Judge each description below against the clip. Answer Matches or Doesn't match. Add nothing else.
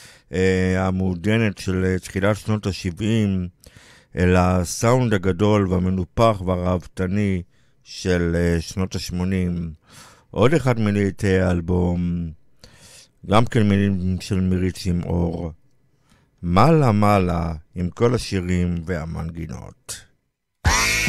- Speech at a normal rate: Doesn't match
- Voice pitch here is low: Matches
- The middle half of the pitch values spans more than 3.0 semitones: Doesn't match